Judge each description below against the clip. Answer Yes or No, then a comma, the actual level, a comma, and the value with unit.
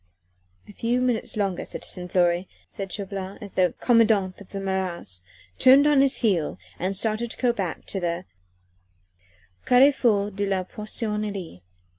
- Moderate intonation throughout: Yes, average, 3.6 semitones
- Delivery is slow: No, average, 145 wpm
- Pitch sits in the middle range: No, high, 200 Hz